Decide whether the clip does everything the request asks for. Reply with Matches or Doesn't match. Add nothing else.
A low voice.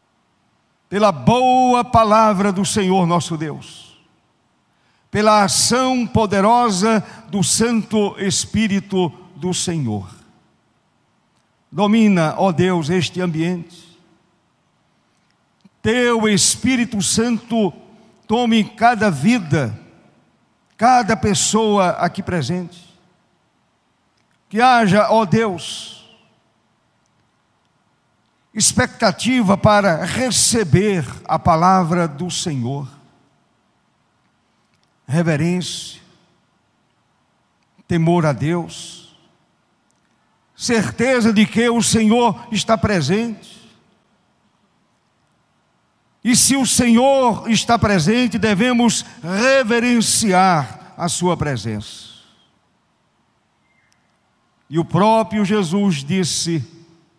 Doesn't match